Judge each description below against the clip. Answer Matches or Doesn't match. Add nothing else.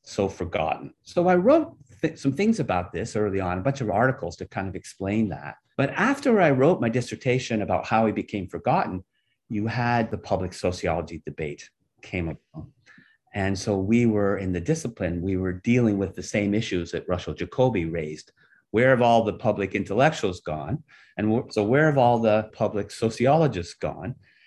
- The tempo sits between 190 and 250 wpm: Doesn't match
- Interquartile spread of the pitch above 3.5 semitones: Matches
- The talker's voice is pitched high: Doesn't match